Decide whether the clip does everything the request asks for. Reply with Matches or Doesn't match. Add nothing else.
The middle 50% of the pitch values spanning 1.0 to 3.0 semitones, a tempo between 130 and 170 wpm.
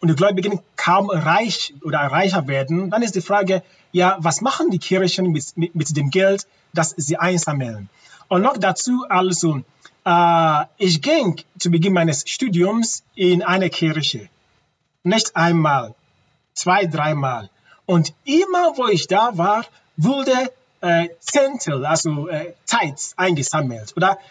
Doesn't match